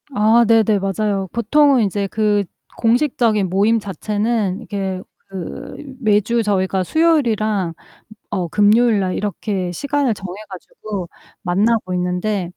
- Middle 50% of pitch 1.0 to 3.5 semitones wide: Yes, average, 3.1 semitones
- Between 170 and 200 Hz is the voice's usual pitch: No, high, 210 Hz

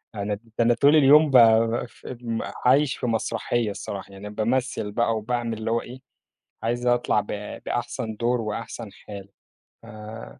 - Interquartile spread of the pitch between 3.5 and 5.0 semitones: No, narrow, 2.5 semitones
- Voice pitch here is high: No, low, 115 Hz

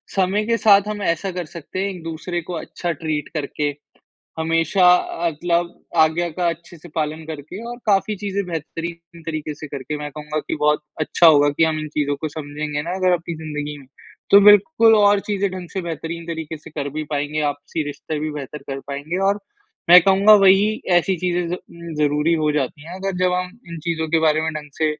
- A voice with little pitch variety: No, average, 3.2 semitones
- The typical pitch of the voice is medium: Yes, medium, 165 Hz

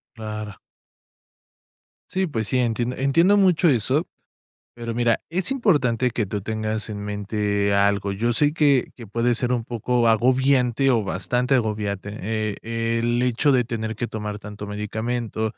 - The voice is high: No, low, 115 Hz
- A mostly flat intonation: No, average, 3.0 semitones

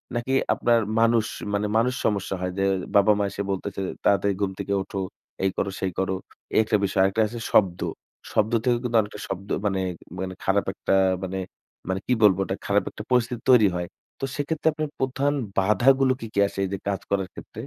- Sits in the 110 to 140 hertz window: No, low, 100 Hz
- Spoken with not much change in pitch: No, average, 3.5 semitones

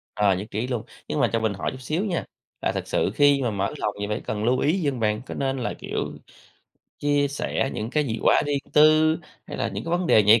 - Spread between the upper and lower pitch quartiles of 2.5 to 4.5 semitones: No, average, 5.3 semitones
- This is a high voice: No, low, 130 Hz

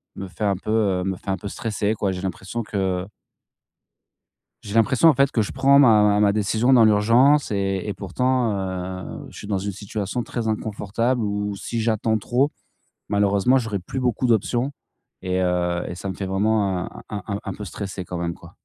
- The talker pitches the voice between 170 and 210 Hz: No, low, 105 Hz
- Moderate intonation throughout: Yes, average, 3.1 semitones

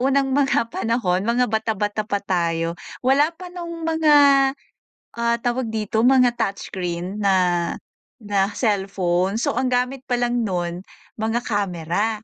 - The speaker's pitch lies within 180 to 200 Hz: No, high, 225 Hz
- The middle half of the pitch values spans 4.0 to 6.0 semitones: Yes, average, 4.6 semitones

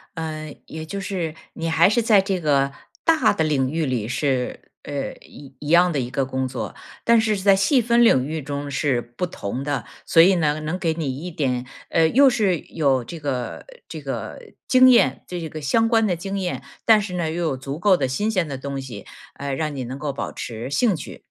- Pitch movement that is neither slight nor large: No, wide, 5.9 semitones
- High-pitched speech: No, medium, 155 Hz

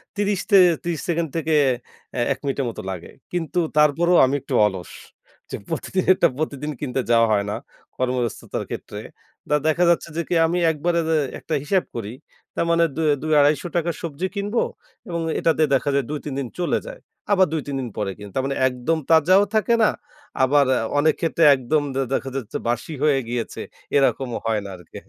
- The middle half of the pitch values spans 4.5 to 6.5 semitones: Yes, average, 4.8 semitones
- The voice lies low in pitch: No, medium, 150 Hz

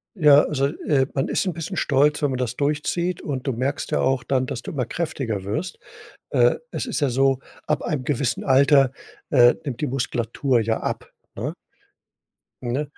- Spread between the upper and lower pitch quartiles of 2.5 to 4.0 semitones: Yes, average, 2.8 semitones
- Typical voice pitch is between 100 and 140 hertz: Yes, low, 135 Hz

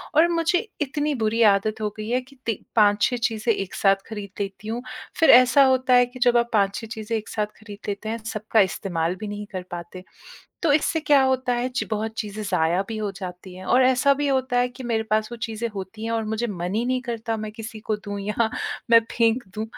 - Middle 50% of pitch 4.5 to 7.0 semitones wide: No, average, 3.2 semitones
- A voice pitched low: No, high, 220 Hz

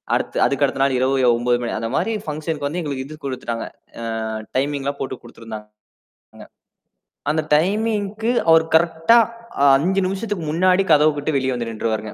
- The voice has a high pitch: No, medium, 145 Hz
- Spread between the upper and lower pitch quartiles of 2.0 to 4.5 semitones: No, wide, 5.4 semitones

